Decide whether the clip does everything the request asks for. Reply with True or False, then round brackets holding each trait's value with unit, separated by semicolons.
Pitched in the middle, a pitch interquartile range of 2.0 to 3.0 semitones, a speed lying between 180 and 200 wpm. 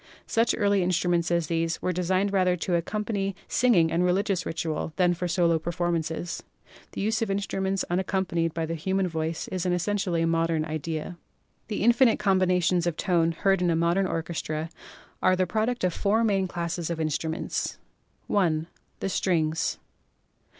False (175 Hz; 2.7 semitones; 165 wpm)